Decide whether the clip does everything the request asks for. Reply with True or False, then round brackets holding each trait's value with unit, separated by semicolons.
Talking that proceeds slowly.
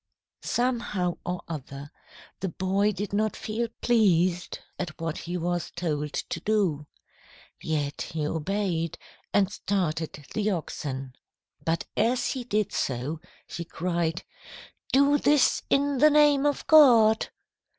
True (125 wpm)